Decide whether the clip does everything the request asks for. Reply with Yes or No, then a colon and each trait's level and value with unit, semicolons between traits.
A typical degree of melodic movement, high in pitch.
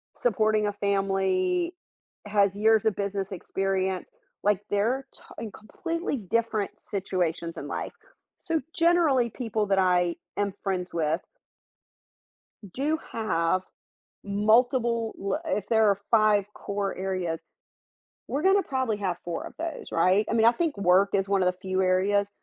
Yes: average, 3.4 semitones; high, 205 Hz